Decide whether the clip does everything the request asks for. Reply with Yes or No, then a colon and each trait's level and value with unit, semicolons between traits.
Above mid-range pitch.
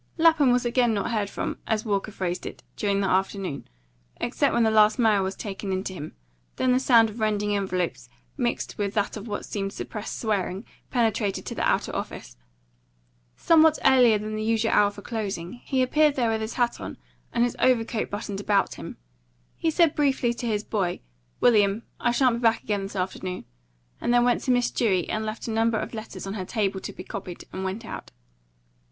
Yes: high, 215 Hz